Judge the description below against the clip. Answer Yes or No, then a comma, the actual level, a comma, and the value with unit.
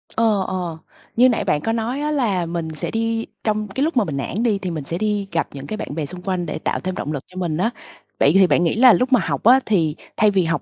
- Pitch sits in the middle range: No, high, 195 Hz